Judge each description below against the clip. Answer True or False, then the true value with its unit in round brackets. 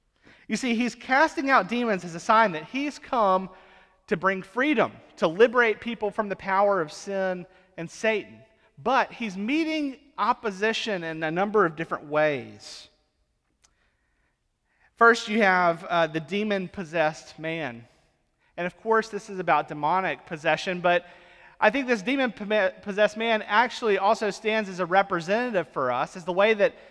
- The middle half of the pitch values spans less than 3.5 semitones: False (4.4 semitones)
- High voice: True (195 Hz)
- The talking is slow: False (155 wpm)